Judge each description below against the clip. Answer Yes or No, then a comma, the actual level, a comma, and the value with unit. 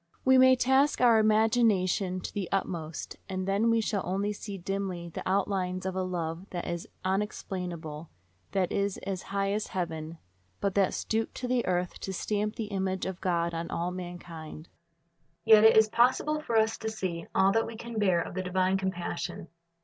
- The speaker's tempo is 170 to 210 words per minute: Yes, average, 185 wpm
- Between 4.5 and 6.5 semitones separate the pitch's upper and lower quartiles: No, average, 3.4 semitones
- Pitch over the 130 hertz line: Yes, high, 190 Hz